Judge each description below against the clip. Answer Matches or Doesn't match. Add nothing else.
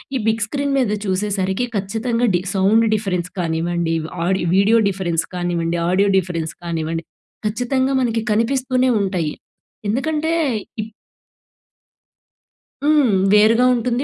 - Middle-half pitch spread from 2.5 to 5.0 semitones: Doesn't match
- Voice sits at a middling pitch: Doesn't match